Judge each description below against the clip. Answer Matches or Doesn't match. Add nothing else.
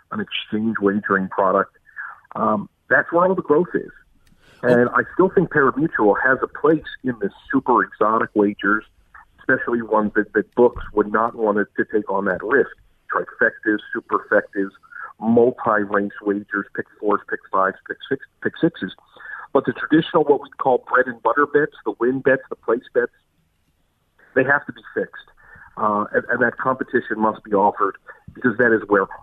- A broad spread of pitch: Matches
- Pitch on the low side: Matches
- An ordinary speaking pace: Matches